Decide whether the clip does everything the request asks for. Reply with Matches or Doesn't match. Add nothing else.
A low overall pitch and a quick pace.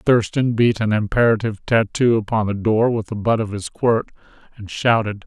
Doesn't match